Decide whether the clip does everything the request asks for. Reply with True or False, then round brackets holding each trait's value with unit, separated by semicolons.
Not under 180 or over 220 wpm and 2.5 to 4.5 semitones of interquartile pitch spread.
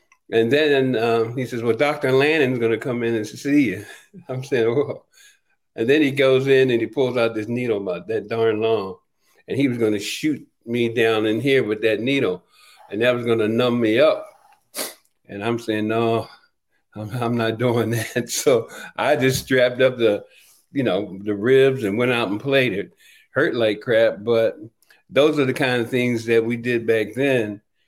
True (200 wpm; 2.9 semitones)